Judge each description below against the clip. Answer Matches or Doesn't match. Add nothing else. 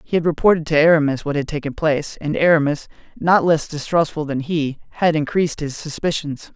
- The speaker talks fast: Doesn't match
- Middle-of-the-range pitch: Matches